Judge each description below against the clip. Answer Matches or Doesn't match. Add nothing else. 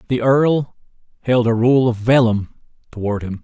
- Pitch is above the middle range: Doesn't match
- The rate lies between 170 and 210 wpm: Doesn't match